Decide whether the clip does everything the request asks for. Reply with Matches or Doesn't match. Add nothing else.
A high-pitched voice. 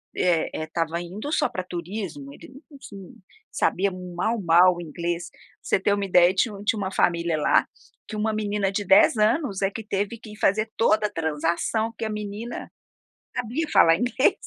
Matches